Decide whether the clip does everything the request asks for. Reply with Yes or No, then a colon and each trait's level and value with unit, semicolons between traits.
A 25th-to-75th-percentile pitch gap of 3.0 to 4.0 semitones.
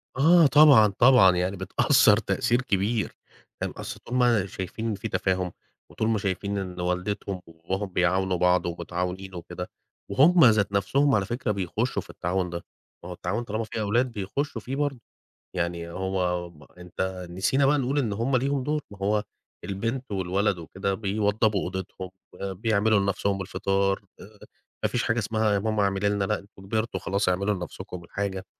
Yes: average, 3.5 semitones